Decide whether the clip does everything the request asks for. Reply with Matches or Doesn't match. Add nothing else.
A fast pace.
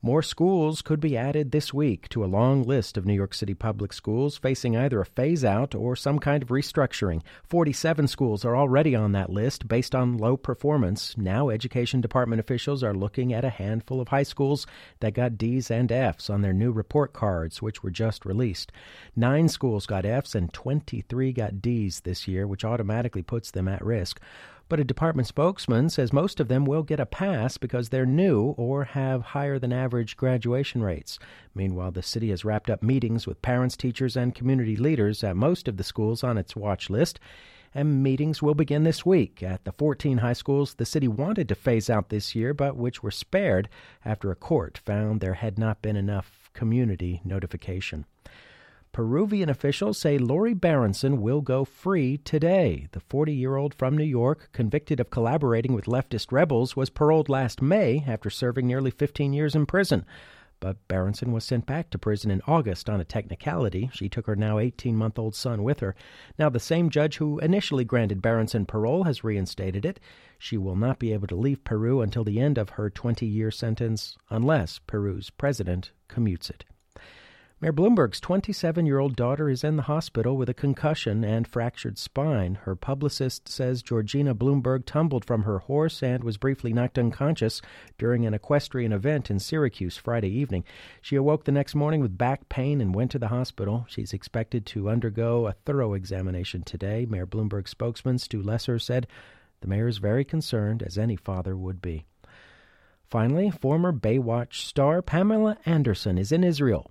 Doesn't match